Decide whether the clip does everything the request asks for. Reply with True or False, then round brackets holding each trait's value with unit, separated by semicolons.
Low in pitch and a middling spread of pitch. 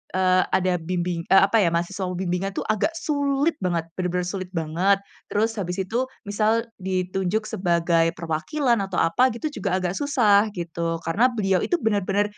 False (190 Hz; 3.7 semitones)